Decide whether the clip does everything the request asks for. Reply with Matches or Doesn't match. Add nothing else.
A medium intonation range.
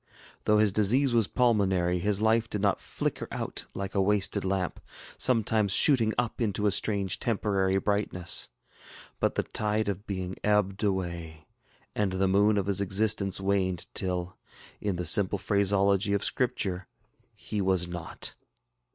Doesn't match